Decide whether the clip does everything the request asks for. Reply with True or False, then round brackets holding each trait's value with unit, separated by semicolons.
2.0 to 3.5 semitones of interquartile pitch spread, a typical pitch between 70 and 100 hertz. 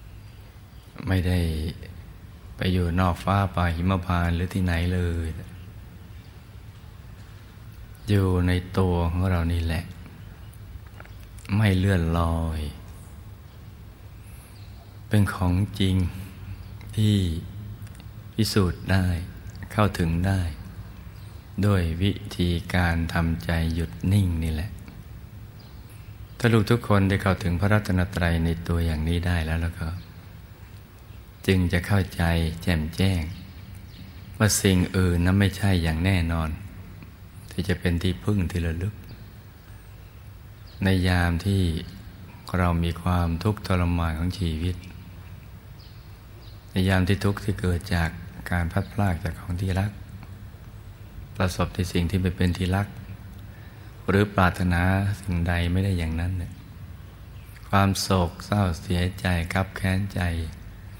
True (2.5 semitones; 95 Hz)